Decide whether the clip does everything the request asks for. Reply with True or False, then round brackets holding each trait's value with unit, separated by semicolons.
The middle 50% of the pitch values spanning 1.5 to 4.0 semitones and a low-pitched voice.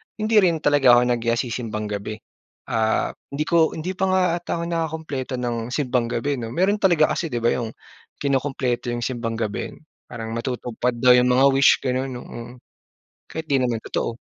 False (4.8 semitones; 125 Hz)